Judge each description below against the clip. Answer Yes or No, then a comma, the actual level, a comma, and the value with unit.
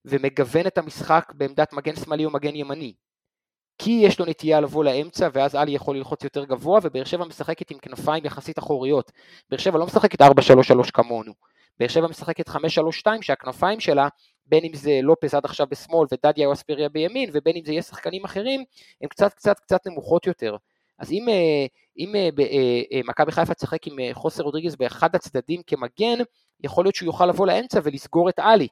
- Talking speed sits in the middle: No, fast, 170 wpm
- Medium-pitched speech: Yes, medium, 155 Hz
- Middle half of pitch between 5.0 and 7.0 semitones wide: No, average, 3.9 semitones